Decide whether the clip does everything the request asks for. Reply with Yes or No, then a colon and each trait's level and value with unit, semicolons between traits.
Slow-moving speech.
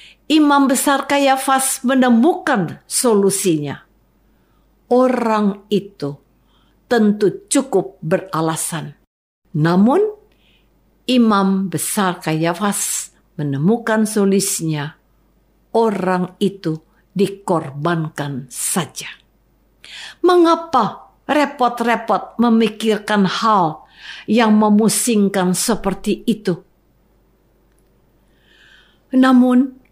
Yes: slow, 60 wpm